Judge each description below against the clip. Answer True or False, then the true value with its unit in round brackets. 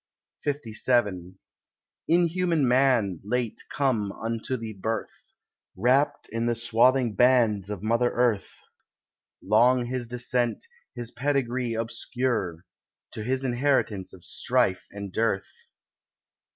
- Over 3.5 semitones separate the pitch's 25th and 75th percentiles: False (3.1 semitones)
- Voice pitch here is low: True (120 Hz)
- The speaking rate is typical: False (105 wpm)